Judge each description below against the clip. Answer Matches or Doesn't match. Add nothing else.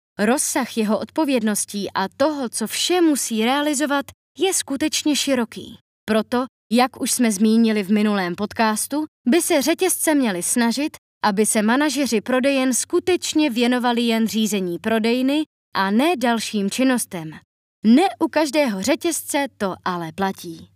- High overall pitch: Matches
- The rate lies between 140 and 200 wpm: Doesn't match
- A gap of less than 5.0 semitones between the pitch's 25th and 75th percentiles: Doesn't match